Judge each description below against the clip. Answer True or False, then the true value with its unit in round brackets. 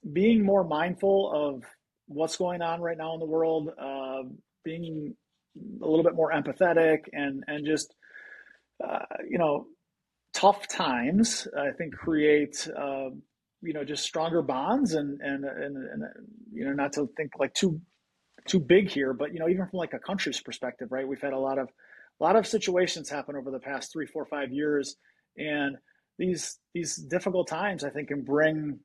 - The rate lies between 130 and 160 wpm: False (180 wpm)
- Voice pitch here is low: False (160 Hz)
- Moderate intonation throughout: True (4.2 semitones)